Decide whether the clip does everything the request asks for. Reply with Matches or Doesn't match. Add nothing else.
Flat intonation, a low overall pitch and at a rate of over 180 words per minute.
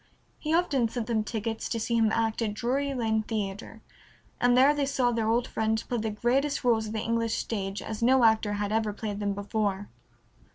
Doesn't match